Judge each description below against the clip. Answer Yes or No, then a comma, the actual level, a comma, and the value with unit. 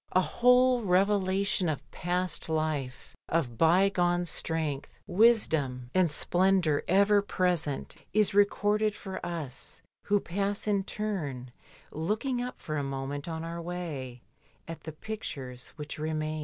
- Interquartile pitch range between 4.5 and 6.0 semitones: Yes, average, 4.9 semitones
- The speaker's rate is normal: No, slow, 130 wpm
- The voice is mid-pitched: Yes, medium, 175 Hz